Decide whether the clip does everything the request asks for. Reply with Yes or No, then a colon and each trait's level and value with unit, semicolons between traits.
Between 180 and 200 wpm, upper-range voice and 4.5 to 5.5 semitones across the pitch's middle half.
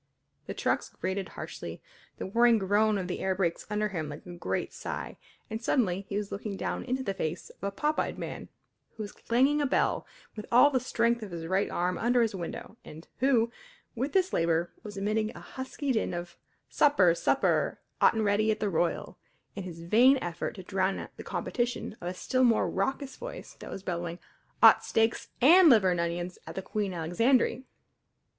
Yes: average, 195 wpm; high, 205 Hz; average, 5.0 semitones